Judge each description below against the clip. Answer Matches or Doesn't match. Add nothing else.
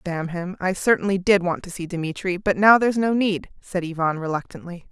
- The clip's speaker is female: Matches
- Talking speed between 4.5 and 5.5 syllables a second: Matches